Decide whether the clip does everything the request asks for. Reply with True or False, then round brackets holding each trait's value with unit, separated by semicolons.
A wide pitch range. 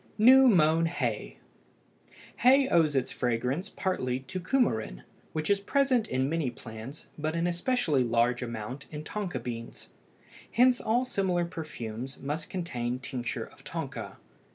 True (7.9 semitones)